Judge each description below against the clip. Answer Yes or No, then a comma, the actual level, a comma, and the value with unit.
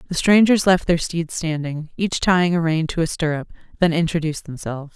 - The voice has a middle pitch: Yes, medium, 165 Hz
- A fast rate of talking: No, average, 195 wpm